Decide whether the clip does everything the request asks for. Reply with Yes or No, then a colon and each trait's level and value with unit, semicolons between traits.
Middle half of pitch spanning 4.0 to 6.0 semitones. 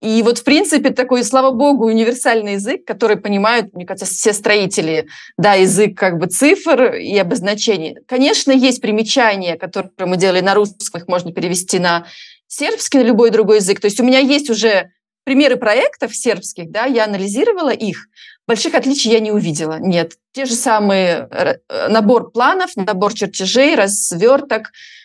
Yes: average, 4.7 semitones